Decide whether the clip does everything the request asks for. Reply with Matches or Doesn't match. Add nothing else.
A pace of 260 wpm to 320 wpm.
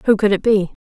Matches